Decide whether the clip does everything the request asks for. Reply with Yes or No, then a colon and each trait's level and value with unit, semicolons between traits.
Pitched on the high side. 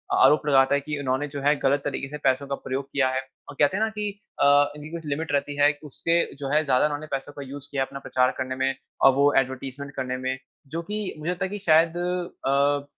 No: medium, 145 Hz